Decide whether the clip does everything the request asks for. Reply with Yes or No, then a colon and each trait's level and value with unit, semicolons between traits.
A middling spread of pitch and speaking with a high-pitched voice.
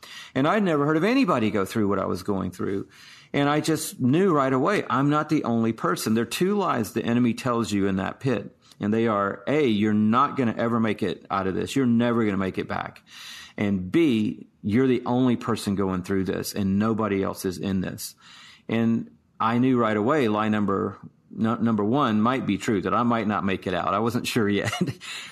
No: average, 3.4 semitones; low, 110 Hz